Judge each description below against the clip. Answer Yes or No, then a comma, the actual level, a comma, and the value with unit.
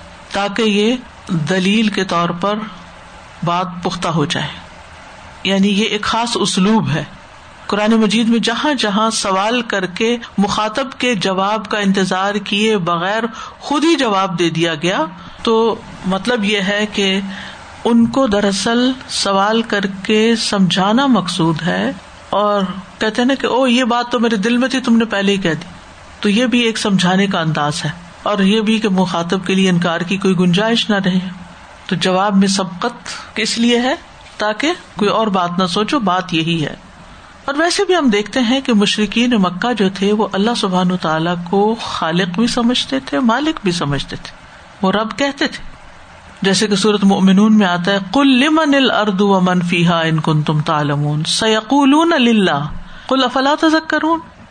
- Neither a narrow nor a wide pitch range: Yes, average, 4.0 semitones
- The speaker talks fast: No, average, 170 wpm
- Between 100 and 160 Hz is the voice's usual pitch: No, high, 205 Hz